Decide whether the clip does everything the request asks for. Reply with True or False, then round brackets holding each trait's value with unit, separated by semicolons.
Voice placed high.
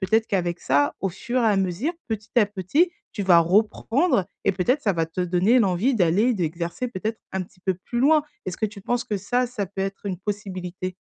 True (200 Hz)